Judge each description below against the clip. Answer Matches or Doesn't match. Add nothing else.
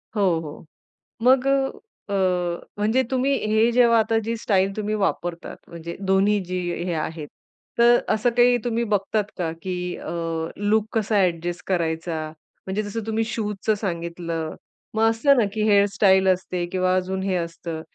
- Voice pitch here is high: Matches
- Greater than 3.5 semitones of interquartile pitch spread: Matches